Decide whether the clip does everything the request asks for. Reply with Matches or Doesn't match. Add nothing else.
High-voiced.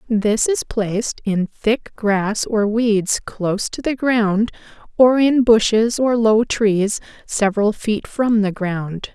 Matches